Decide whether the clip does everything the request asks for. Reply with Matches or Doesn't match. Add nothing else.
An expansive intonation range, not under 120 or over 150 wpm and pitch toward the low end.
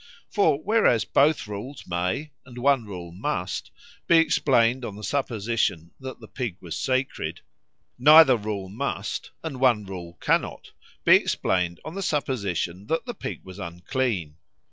Matches